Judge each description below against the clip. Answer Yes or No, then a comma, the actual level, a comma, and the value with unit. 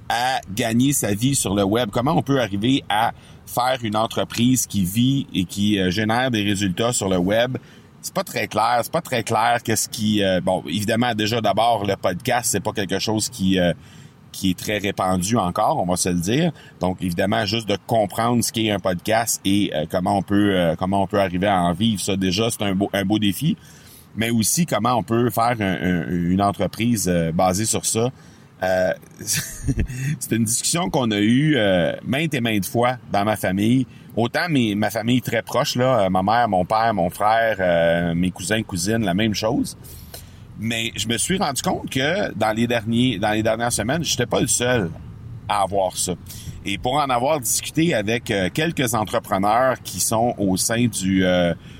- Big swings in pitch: No, average, 3.8 semitones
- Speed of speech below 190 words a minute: No, average, 200 wpm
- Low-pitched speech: Yes, low, 110 Hz